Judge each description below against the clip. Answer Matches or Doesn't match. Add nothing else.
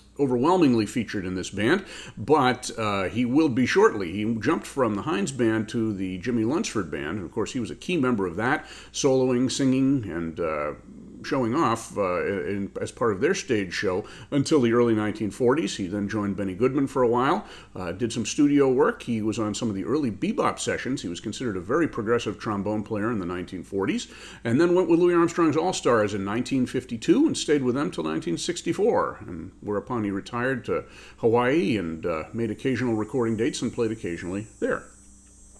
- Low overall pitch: Matches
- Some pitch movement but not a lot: Matches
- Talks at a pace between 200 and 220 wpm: Doesn't match